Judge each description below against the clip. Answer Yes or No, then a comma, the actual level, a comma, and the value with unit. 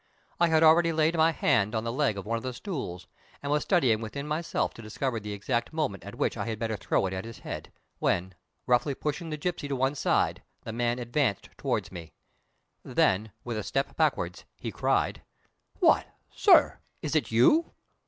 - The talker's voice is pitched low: Yes, low, 125 Hz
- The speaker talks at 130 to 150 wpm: No, average, 195 wpm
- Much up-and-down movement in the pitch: Yes, wide, 5.9 semitones